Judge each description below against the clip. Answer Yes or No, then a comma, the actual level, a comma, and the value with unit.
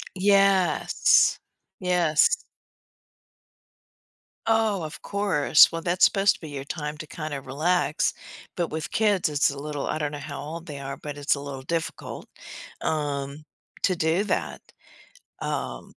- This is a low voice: No, medium, 155 Hz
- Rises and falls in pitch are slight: No, average, 3.9 semitones